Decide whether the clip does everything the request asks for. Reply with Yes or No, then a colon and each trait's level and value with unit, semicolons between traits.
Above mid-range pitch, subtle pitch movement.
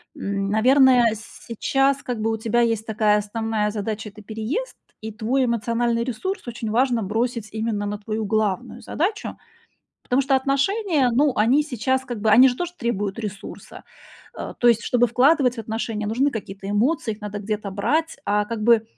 No: high, 230 Hz; average, 3.4 semitones